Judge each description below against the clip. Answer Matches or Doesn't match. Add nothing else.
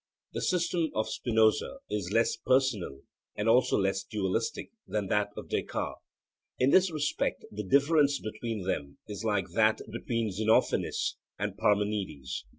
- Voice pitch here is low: Matches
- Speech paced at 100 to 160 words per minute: Matches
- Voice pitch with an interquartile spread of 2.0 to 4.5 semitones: Matches